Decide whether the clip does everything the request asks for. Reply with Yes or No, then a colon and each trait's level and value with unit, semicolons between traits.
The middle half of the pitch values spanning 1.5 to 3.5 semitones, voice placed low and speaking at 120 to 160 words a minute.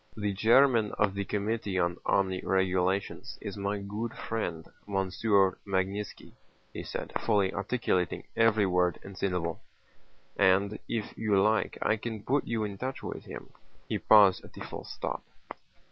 Yes: narrow, 2.5 semitones; low, 100 Hz; average, 150 wpm